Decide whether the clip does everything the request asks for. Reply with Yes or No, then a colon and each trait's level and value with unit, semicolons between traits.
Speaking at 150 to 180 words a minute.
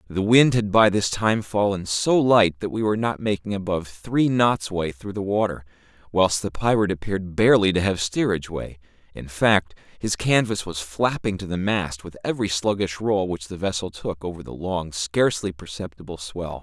No: average, 190 wpm